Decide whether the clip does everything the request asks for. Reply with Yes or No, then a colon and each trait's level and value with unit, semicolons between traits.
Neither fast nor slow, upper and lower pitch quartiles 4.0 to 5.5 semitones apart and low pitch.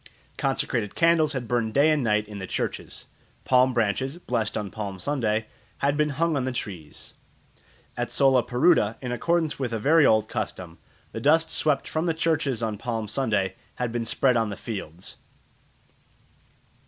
Yes: average, 165 wpm; average, 5.1 semitones; low, 120 Hz